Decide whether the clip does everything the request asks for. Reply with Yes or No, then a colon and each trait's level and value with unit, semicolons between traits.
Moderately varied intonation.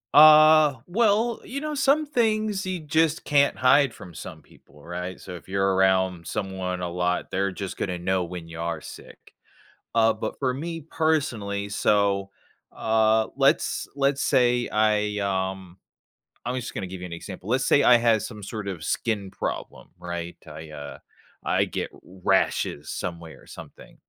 No: wide, 7.6 semitones